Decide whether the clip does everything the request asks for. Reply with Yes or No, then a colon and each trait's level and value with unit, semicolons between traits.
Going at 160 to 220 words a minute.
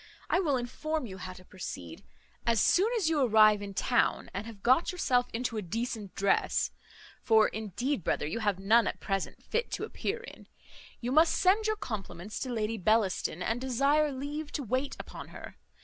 Yes: average, 185 wpm